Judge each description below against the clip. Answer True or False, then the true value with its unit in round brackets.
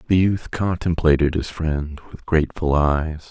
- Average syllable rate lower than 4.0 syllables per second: False (4.2 syllables/s)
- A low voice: True (80 Hz)